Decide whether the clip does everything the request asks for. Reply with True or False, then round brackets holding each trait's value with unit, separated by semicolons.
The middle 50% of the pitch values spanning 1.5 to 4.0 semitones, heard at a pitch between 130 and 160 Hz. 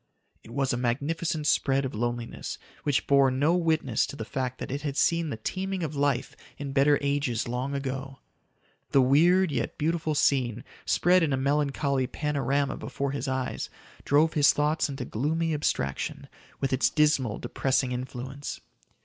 True (2.5 semitones; 140 Hz)